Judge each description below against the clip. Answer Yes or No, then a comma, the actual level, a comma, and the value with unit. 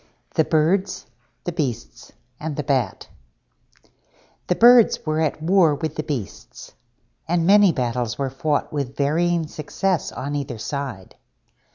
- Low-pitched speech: No, medium, 150 Hz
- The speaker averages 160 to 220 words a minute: No, slow, 135 wpm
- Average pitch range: Yes, average, 4.1 semitones